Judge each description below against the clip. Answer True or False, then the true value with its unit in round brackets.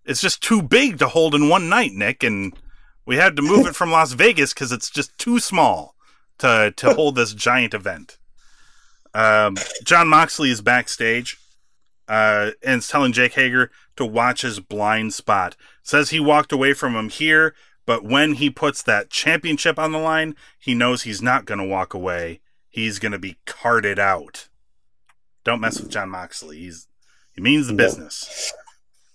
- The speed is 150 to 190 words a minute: True (175 wpm)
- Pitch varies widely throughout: True (6.0 semitones)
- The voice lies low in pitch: True (125 Hz)